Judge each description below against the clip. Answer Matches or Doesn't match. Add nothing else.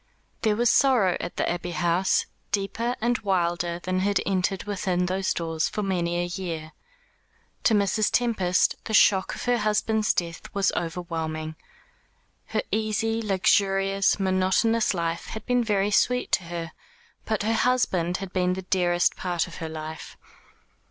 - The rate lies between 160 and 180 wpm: Doesn't match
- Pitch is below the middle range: Doesn't match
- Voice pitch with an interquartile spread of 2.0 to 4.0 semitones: Matches